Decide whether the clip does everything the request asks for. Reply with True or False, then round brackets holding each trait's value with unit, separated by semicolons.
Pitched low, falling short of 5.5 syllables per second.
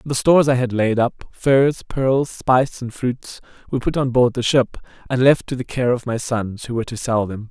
True (125 Hz; 5.0 syllables/s)